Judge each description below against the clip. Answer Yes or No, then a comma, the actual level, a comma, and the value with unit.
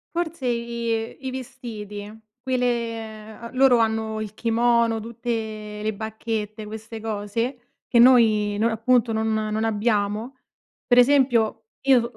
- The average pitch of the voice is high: Yes, high, 225 Hz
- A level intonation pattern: Yes, narrow, 1.9 semitones